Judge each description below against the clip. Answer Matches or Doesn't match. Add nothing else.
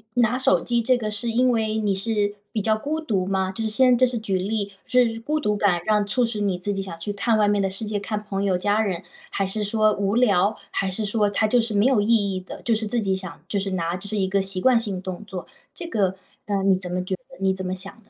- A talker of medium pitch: Doesn't match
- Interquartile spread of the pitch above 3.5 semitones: Doesn't match